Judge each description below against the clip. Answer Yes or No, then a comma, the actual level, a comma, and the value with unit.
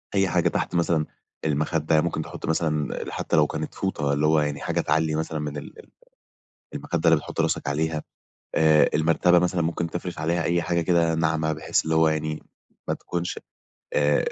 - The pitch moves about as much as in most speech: No, narrow, 1.7 semitones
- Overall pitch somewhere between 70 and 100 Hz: Yes, very low, 80 Hz